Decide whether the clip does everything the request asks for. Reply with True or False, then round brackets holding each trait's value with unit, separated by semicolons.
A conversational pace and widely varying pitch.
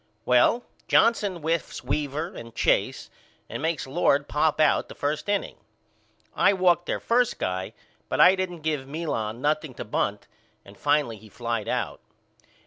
True (150 wpm; 6.1 semitones)